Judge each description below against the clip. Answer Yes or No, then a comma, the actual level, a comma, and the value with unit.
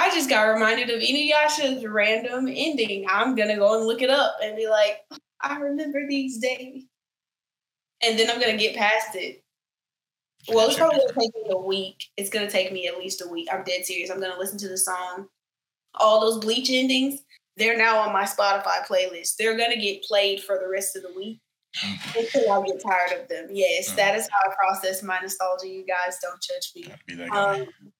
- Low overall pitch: No, high, 215 Hz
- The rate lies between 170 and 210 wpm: Yes, average, 200 wpm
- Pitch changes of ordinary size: Yes, average, 5.0 semitones